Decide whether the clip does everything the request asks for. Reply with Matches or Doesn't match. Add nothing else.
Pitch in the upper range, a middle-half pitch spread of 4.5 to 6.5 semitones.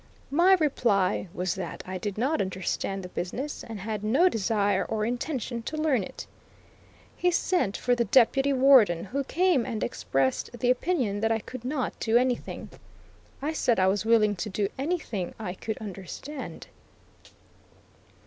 Matches